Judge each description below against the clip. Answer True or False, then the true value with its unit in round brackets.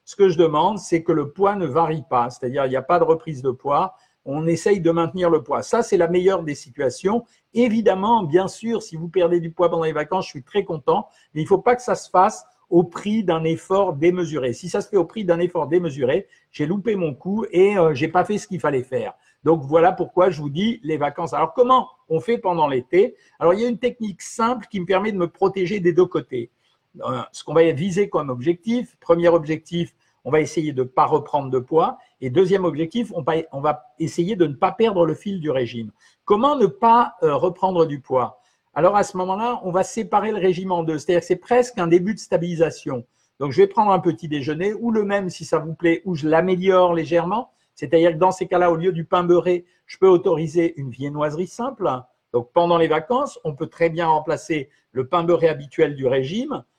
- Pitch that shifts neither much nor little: True (3.5 semitones)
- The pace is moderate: False (230 wpm)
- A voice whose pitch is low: False (175 Hz)